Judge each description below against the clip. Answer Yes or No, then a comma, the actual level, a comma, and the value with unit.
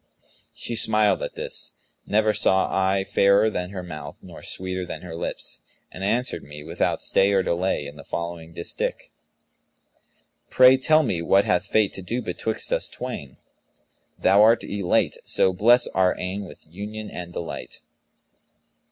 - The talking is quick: No, average, 155 wpm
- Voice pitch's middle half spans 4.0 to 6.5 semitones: No, average, 3.5 semitones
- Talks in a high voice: No, very low, 95 Hz